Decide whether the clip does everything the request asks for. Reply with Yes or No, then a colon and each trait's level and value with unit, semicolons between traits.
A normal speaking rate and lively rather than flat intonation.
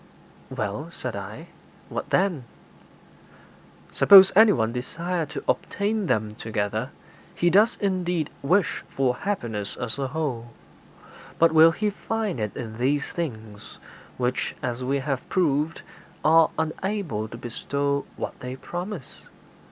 No: slow, 125 wpm; wide, 6.9 semitones